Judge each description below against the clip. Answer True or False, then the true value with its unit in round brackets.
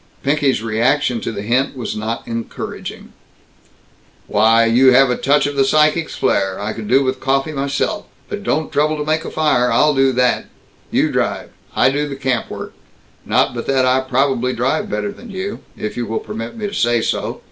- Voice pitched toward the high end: False (135 Hz)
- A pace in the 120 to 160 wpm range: False (195 wpm)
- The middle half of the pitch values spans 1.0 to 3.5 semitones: False (3.9 semitones)